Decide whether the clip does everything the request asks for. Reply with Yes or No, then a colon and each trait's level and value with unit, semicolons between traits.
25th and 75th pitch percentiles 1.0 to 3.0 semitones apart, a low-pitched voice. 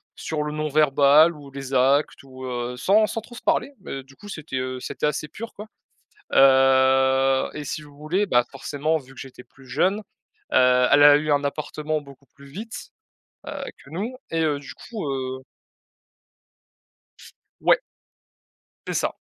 No: average, 2.7 semitones; medium, 145 Hz